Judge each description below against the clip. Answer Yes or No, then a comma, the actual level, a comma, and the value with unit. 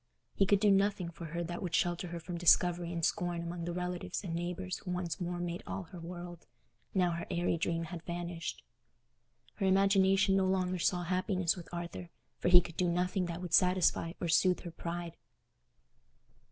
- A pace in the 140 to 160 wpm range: No, average, 190 wpm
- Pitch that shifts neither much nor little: No, narrow, 1.3 semitones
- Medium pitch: Yes, medium, 175 Hz